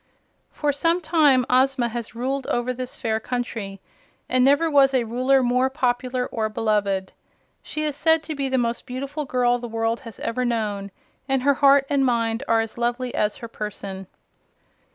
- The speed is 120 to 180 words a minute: Yes, average, 175 wpm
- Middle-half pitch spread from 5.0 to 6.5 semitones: No, average, 3.0 semitones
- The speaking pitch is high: Yes, very high, 250 Hz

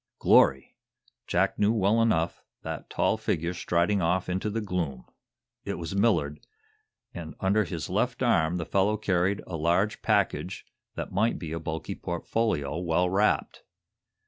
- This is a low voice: Yes, very low, 90 Hz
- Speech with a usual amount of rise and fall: Yes, average, 3.6 semitones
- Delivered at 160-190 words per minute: No, average, 145 wpm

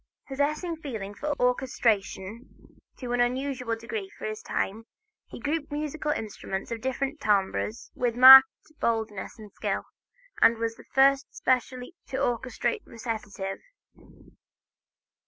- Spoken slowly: Yes, slow, 120 wpm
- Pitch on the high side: Yes, high, 245 Hz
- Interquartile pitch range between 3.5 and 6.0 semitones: Yes, average, 3.9 semitones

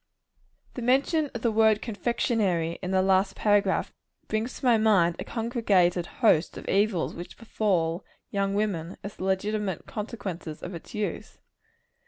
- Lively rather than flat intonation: No, average, 3.5 semitones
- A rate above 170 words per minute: No, average, 150 wpm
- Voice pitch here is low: No, high, 205 Hz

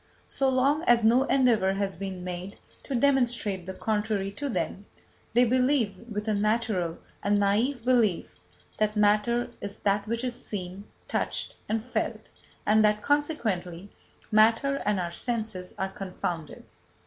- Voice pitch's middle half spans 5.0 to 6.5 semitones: No, average, 3.7 semitones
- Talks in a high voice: Yes, high, 215 Hz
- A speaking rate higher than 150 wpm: No, average, 145 wpm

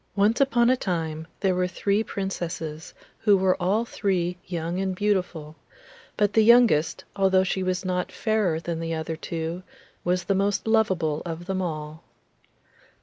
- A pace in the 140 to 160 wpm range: Yes, average, 155 wpm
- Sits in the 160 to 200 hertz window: Yes, medium, 185 Hz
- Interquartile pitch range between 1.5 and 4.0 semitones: Yes, average, 3.4 semitones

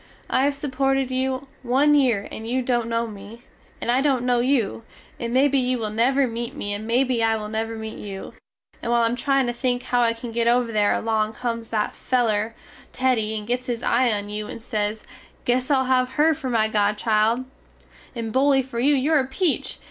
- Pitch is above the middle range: Yes, high, 240 Hz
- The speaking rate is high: Yes, fast, 210 wpm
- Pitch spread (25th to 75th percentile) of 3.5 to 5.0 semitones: No, average, 2.8 semitones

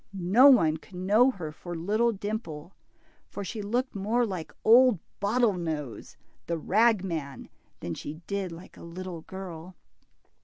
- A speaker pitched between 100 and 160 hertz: No, high, 190 Hz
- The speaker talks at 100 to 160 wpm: Yes, average, 140 wpm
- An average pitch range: Yes, average, 4.7 semitones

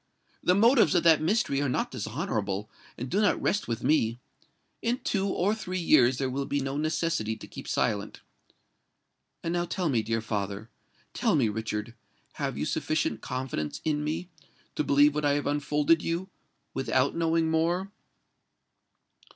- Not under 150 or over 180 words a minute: Yes, average, 155 wpm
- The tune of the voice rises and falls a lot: Yes, wide, 6.1 semitones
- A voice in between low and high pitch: Yes, medium, 145 Hz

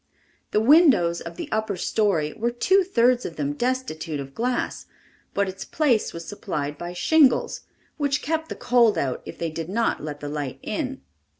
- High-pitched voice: Yes, high, 215 Hz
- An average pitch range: No, wide, 8.1 semitones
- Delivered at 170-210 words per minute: Yes, average, 180 wpm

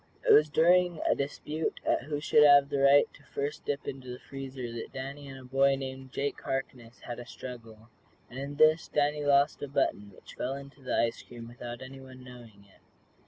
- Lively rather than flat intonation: No, narrow, 2.5 semitones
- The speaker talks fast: Yes, fast, 210 wpm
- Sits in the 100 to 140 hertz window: Yes, low, 135 Hz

